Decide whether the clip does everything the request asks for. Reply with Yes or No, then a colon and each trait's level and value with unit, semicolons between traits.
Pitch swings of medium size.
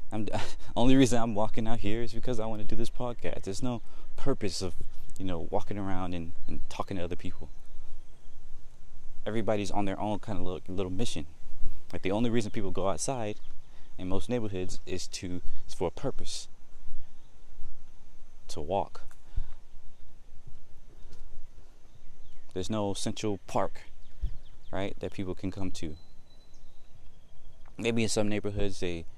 Yes: average, 3.4 semitones